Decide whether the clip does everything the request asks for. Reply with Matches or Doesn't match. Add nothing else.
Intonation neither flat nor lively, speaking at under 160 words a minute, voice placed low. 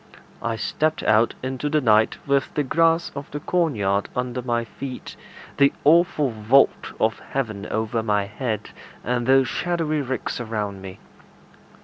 Matches